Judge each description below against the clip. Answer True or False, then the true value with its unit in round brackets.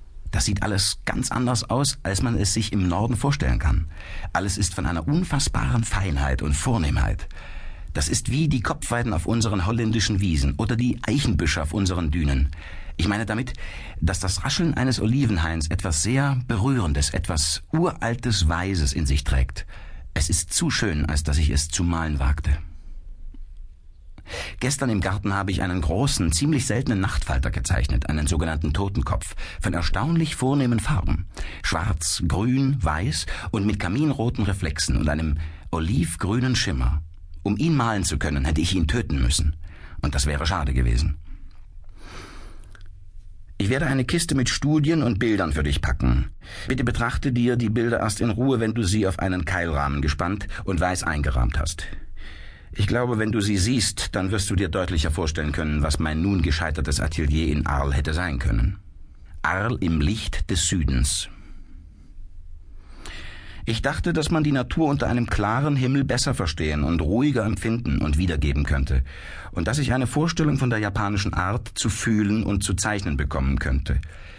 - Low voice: True (90 Hz)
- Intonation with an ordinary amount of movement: False (6.3 semitones)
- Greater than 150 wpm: True (160 wpm)